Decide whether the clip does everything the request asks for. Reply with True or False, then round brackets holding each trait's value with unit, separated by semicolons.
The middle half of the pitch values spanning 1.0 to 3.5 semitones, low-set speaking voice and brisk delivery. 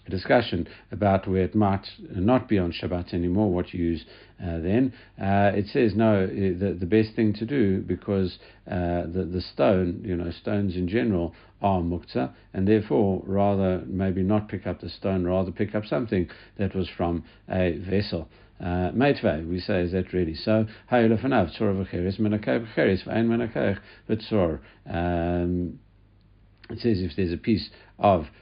False (3.1 semitones; 95 Hz; 150 wpm)